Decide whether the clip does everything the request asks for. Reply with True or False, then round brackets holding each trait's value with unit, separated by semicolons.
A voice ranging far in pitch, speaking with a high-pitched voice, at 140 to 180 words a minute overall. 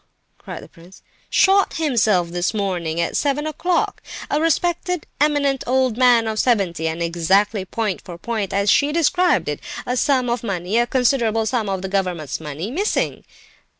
True (7.1 semitones; 225 Hz; 160 wpm)